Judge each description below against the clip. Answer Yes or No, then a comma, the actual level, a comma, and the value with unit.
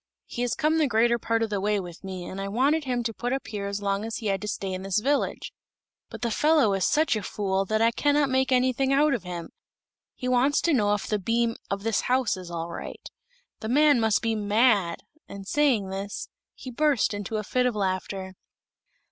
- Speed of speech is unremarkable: No, fast, 225 wpm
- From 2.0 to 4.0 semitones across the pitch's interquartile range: No, average, 4.5 semitones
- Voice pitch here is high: Yes, high, 220 Hz